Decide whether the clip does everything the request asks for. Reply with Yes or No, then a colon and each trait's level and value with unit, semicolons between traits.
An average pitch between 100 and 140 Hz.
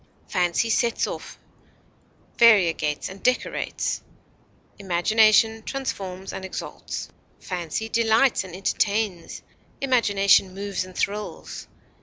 No: high, 200 Hz